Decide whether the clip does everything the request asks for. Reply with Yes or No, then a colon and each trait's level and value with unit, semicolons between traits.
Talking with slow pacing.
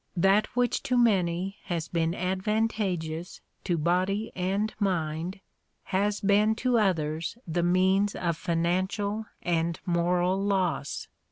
Yes: slow, 115 wpm